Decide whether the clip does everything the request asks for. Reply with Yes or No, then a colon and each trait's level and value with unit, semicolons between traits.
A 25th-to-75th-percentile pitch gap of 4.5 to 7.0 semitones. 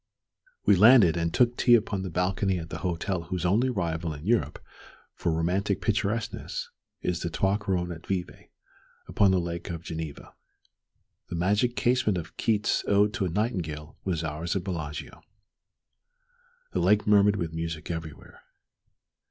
No: average, 3.7 semitones